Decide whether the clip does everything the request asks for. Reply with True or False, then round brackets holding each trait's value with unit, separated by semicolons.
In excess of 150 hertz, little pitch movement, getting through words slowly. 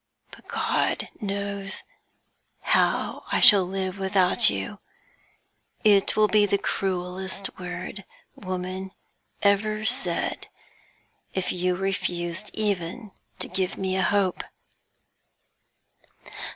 True (190 Hz; 1.8 semitones; 100 wpm)